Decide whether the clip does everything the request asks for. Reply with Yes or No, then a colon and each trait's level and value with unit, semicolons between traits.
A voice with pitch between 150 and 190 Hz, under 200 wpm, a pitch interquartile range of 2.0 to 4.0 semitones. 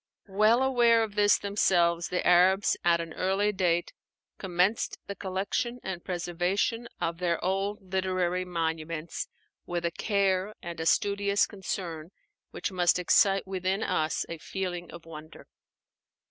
Yes: medium, 185 Hz; slow, 135 wpm; average, 2.7 semitones